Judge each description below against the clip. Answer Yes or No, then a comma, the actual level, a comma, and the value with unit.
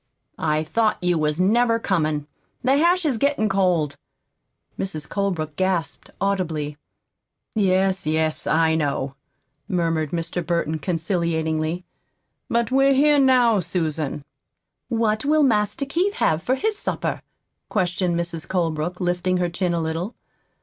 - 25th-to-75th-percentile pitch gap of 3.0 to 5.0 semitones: No, wide, 5.5 semitones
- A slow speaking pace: Yes, slow, 130 wpm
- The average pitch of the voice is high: No, medium, 180 Hz